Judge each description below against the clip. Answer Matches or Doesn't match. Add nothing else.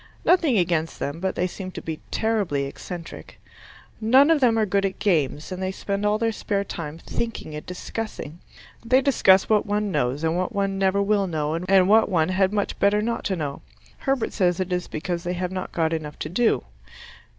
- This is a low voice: Doesn't match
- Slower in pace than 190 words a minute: Doesn't match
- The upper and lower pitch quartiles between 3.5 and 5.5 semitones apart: Matches